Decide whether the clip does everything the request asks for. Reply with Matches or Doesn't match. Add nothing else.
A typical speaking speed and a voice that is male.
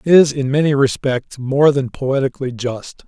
Matches